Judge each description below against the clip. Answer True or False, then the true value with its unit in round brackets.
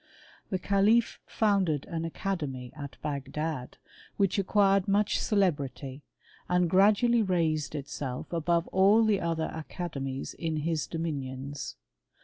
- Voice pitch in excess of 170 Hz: False (165 Hz)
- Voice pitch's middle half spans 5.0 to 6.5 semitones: True (5.3 semitones)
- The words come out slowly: True (115 wpm)